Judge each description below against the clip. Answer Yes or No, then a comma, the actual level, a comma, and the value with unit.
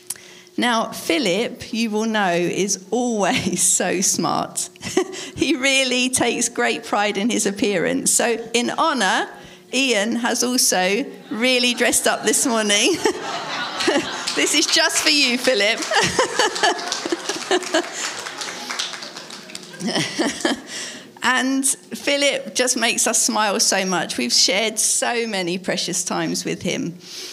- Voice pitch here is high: Yes, high, 245 Hz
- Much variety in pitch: Yes, wide, 5.8 semitones